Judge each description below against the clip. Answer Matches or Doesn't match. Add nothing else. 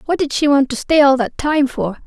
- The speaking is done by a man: Doesn't match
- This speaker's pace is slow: Doesn't match